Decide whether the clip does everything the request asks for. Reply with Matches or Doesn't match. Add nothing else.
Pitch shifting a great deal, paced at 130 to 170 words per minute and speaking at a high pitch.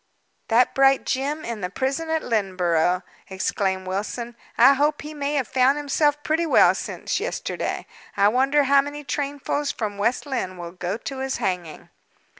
Matches